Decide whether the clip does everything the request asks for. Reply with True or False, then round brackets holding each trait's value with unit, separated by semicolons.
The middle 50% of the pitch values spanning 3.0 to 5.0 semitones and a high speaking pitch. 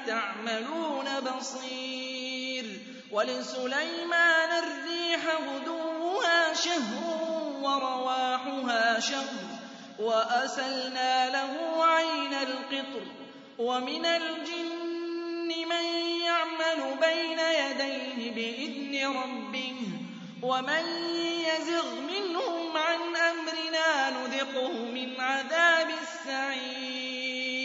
True (4.1 semitones; 275 Hz)